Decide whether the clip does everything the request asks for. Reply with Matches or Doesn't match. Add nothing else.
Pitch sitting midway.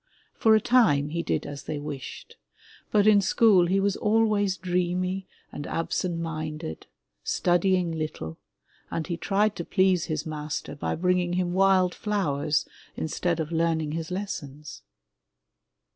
Matches